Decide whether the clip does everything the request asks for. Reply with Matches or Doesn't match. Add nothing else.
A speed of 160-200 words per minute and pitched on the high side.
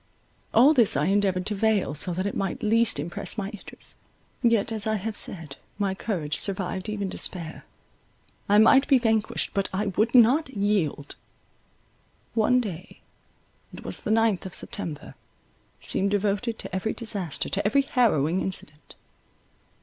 Doesn't match